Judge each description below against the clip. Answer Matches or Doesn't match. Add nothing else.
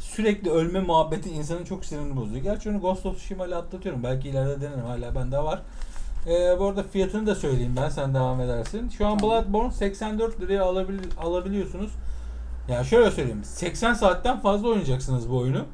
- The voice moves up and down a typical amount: Doesn't match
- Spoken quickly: Matches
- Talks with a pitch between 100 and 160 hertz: Doesn't match